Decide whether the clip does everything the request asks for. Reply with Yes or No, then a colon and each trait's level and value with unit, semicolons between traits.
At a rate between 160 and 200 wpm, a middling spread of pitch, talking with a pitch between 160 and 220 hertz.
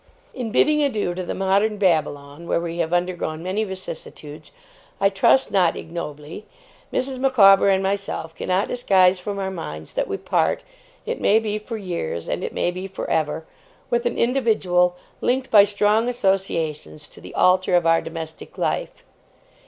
Yes: average, 165 wpm; average, 3.9 semitones; high, 190 Hz